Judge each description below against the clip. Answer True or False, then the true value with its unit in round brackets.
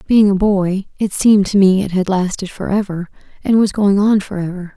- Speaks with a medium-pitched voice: False (195 Hz)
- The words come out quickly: True (225 wpm)